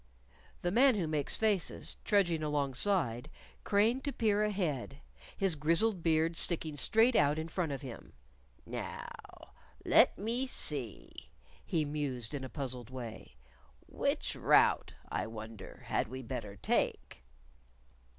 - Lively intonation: Yes, wide, 7.4 semitones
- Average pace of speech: No, slow, 130 wpm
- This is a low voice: No, medium, 155 Hz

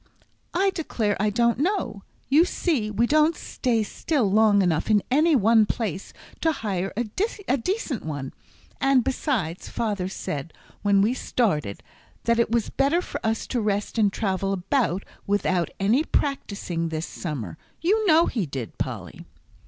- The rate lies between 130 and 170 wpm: Yes, average, 150 wpm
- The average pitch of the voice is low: No, high, 220 Hz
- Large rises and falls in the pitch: Yes, wide, 6.1 semitones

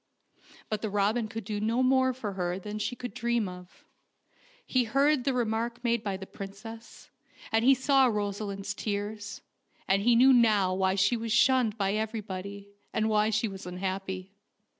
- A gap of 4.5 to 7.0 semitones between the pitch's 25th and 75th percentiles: No, average, 3.2 semitones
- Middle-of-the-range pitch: No, high, 215 Hz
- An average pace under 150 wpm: No, average, 175 wpm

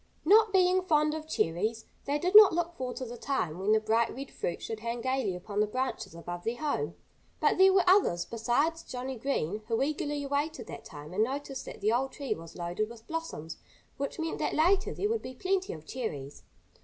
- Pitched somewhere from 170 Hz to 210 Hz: No, very high, 260 Hz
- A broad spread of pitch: Yes, wide, 6.8 semitones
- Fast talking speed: Yes, fast, 210 wpm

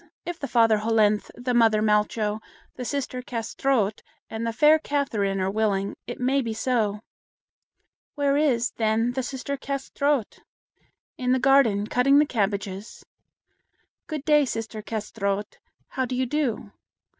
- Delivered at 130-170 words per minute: Yes, average, 140 wpm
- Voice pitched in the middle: No, high, 235 Hz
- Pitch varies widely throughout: No, average, 4.2 semitones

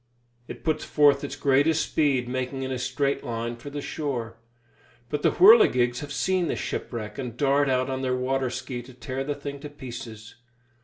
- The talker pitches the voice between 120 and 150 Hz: Yes, low, 135 Hz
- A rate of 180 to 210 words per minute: Yes, average, 190 wpm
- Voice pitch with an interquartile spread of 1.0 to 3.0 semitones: Yes, narrow, 2.6 semitones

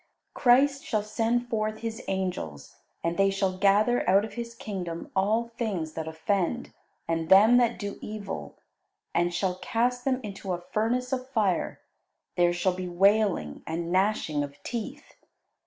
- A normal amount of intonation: Yes, average, 4.7 semitones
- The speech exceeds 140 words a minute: Yes, average, 155 wpm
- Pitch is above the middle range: Yes, high, 200 Hz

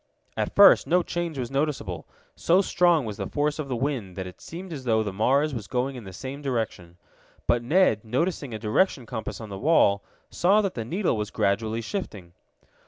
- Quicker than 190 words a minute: Yes, average, 200 wpm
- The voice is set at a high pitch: No, low, 130 Hz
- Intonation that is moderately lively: No, wide, 6.6 semitones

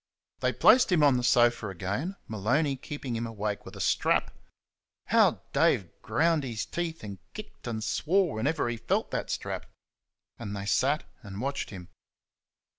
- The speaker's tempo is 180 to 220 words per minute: No, average, 160 wpm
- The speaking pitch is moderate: No, low, 120 Hz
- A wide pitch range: Yes, wide, 6.0 semitones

